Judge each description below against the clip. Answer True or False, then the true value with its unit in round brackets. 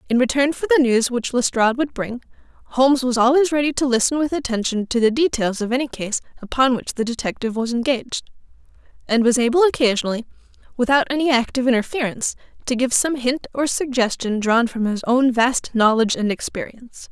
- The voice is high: True (250 Hz)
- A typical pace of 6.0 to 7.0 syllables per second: True (6.1 syllables/s)